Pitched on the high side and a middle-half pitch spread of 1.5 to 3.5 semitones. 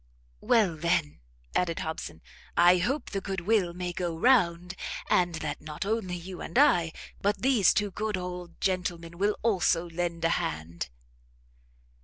No: medium, 180 Hz; average, 3.0 semitones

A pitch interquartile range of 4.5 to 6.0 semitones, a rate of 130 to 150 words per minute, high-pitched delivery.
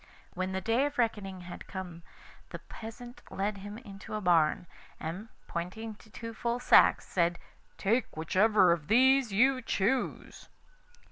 No: average, 4.1 semitones; average, 145 wpm; high, 205 Hz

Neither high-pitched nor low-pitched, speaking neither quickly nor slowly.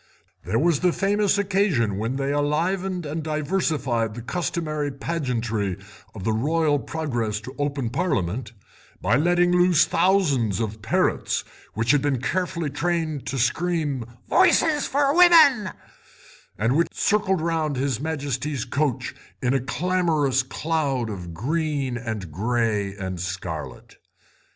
No: medium, 145 Hz; slow, 130 wpm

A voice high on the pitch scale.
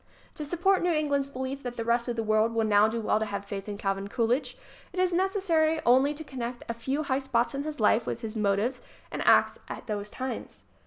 Yes: high, 245 Hz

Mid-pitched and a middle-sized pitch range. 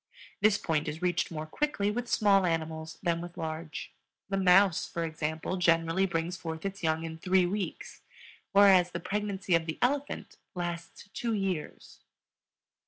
Yes: medium, 175 Hz; average, 3.2 semitones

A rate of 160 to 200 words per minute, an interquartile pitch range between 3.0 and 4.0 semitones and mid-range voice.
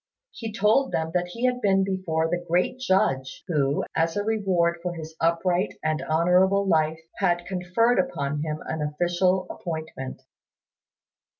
No: average, 145 wpm; average, 3.3 semitones; medium, 175 Hz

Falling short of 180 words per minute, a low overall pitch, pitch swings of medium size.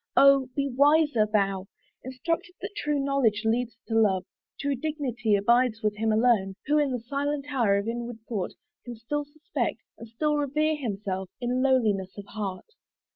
No: average, 165 wpm; high, 245 Hz; average, 4.9 semitones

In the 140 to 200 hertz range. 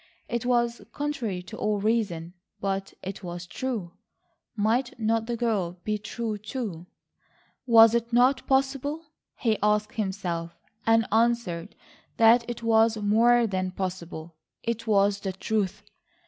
No: high, 220 Hz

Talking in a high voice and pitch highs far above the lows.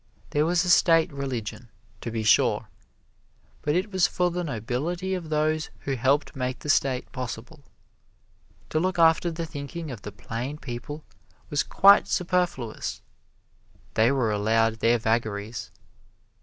No: medium, 140 Hz; wide, 6.0 semitones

